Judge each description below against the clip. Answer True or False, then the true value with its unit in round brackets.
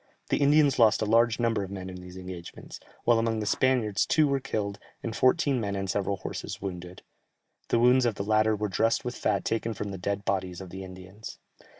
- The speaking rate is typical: False (215 wpm)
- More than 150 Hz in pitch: False (105 Hz)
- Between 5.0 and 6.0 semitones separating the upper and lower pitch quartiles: False (3.6 semitones)